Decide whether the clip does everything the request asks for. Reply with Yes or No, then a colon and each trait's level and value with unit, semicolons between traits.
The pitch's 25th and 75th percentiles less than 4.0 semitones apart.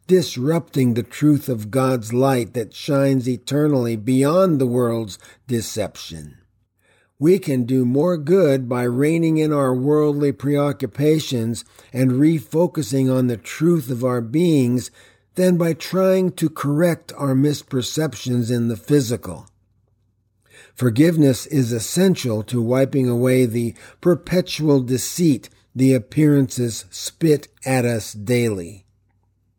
No: average, 4.3 semitones